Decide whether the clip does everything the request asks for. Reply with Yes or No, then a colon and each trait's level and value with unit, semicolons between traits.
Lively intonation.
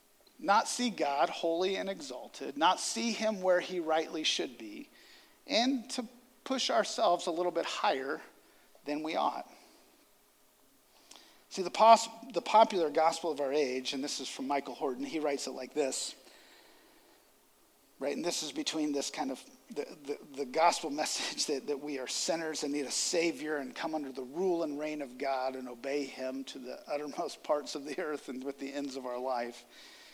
Yes: wide, 7.0 semitones